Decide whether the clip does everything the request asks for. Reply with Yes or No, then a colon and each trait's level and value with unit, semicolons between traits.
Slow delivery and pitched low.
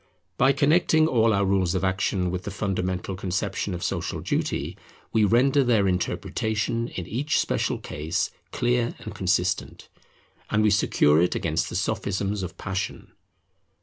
No: average, 150 wpm; low, 100 Hz